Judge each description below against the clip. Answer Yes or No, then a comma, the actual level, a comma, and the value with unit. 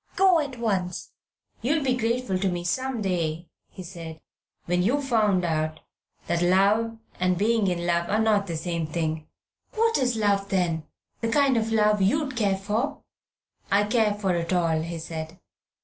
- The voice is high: Yes, high, 195 Hz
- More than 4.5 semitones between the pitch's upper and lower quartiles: Yes, average, 4.9 semitones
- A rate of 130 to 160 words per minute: No, average, 170 wpm